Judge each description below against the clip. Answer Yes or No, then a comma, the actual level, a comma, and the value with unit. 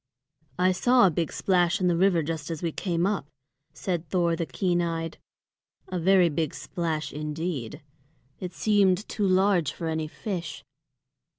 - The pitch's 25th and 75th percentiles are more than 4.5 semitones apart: No, narrow, 2.4 semitones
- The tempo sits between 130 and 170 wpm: Yes, average, 160 wpm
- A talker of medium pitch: Yes, medium, 175 Hz